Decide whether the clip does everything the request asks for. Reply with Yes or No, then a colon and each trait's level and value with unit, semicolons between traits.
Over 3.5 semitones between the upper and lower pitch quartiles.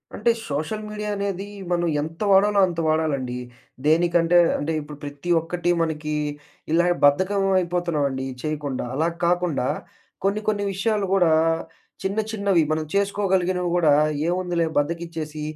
Yes: average, 4.0 semitones